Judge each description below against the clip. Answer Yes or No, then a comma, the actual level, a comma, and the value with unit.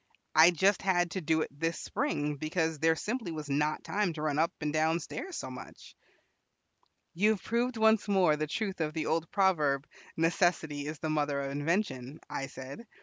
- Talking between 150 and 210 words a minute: Yes, average, 190 wpm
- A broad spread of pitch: No, average, 4.2 semitones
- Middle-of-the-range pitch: Yes, medium, 160 Hz